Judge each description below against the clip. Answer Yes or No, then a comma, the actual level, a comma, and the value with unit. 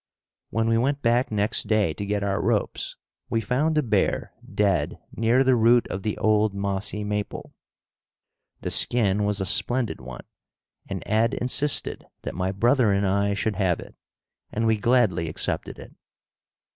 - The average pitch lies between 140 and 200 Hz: No, low, 105 Hz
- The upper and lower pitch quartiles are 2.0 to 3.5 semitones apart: Yes, average, 3.0 semitones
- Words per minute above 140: Yes, average, 160 wpm